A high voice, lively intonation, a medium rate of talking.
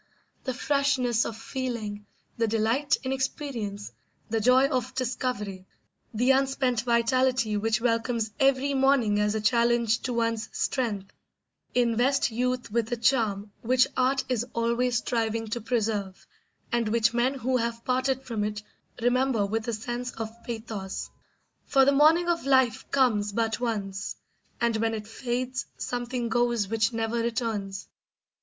No: high, 235 Hz; narrow, 2.6 semitones; average, 145 wpm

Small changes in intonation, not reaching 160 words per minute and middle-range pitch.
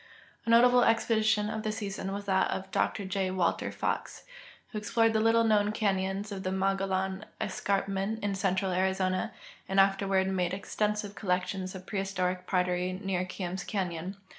No: narrow, 1.9 semitones; average, 150 wpm; high, 195 Hz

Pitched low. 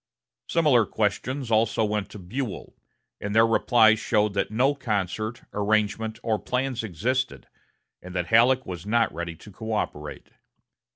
Yes: low, 110 Hz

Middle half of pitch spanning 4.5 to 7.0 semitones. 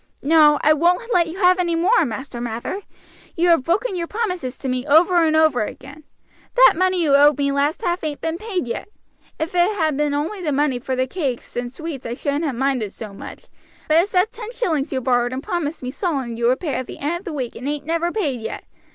Yes: average, 4.9 semitones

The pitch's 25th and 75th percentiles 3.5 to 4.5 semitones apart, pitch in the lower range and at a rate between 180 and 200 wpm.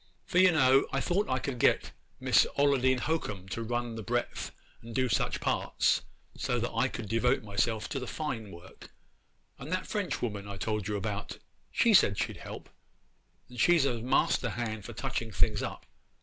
Yes: average, 4.2 semitones; low, 120 Hz; average, 185 wpm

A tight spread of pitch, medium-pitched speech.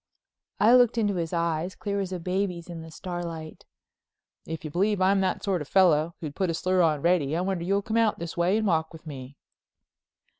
No: average, 3.2 semitones; medium, 175 Hz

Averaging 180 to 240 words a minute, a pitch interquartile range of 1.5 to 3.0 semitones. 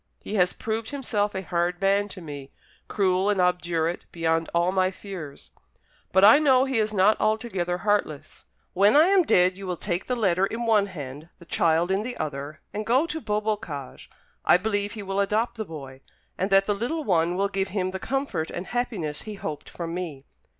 No: average, 200 wpm; average, 3.8 semitones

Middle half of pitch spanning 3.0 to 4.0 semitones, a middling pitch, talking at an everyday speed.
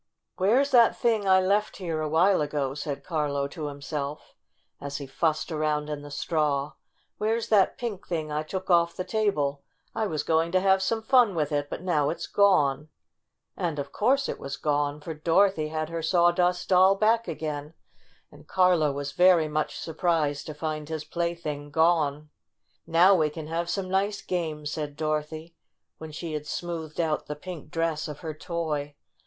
Yes: average, 3.6 semitones; medium, 160 Hz; average, 180 wpm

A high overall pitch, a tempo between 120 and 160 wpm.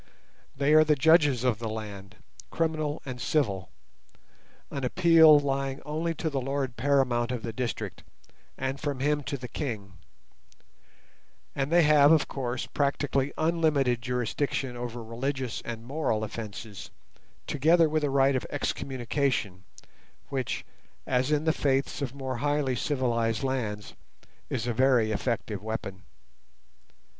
No: low, 135 Hz; slow, 135 wpm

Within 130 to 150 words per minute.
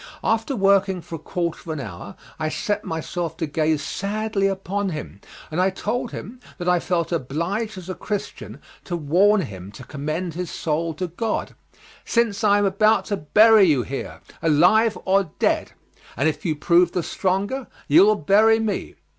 No: average, 180 wpm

